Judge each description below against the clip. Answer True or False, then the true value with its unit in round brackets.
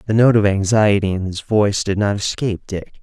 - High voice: False (100 Hz)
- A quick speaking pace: True (220 wpm)